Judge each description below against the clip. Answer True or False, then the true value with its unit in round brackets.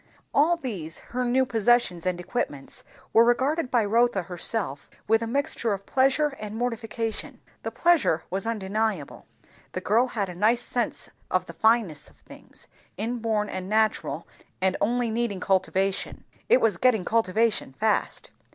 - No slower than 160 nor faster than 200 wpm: False (150 wpm)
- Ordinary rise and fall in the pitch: True (4.1 semitones)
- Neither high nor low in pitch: False (220 Hz)